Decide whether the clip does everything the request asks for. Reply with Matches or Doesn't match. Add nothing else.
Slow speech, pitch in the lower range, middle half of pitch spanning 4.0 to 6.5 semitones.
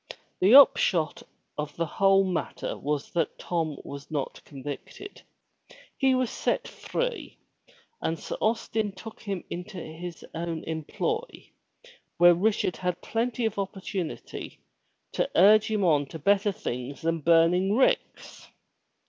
Doesn't match